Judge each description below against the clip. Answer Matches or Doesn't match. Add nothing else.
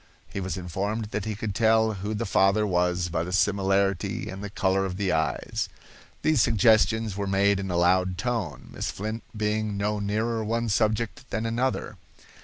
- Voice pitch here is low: Matches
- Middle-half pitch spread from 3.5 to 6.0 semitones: Doesn't match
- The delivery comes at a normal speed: Matches